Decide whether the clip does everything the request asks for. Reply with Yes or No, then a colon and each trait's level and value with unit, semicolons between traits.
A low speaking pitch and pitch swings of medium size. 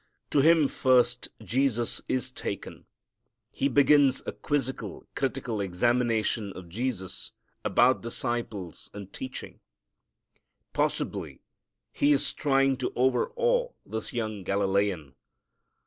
Yes: low, 125 Hz; average, 4.7 semitones